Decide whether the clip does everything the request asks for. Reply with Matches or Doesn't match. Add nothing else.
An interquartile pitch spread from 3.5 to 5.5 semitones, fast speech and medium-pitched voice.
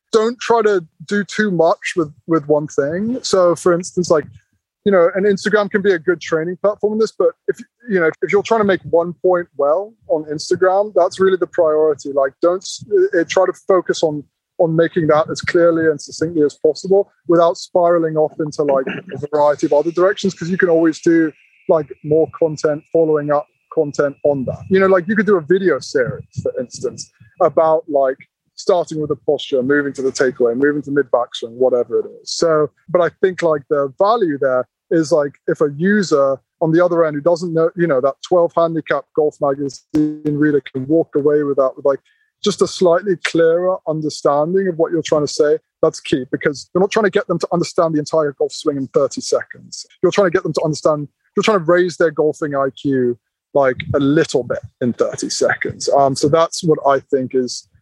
Matches